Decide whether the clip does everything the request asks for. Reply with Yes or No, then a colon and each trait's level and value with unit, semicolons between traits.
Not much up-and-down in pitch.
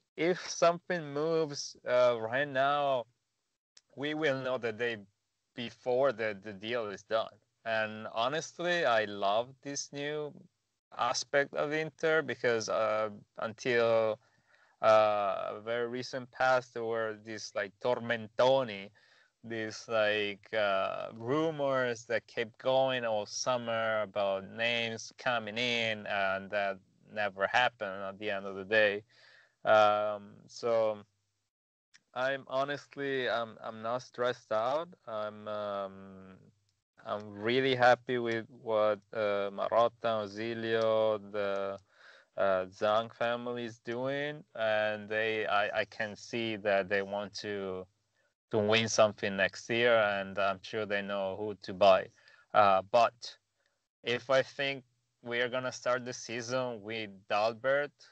No: average, 3.2 semitones